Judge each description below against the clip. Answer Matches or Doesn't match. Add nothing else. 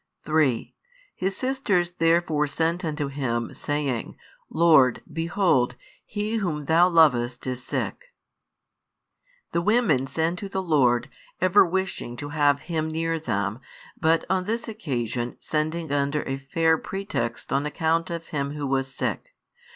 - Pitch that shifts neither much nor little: Matches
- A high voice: Doesn't match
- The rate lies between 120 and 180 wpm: Matches